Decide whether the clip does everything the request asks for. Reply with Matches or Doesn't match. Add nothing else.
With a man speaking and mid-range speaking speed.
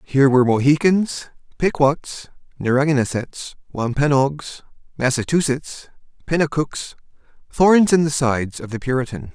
Doesn't match